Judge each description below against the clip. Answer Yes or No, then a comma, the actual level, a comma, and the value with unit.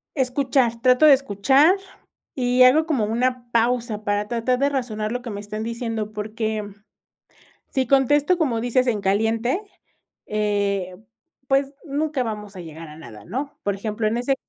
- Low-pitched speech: No, high, 235 Hz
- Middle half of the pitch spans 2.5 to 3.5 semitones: No, average, 3.9 semitones